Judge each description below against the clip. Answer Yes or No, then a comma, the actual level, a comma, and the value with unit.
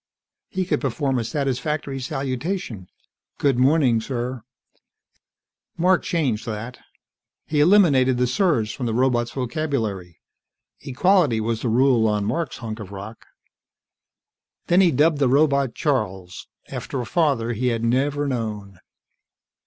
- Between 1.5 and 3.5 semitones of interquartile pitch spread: No, average, 4.3 semitones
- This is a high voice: No, low, 130 Hz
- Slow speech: Yes, slow, 130 wpm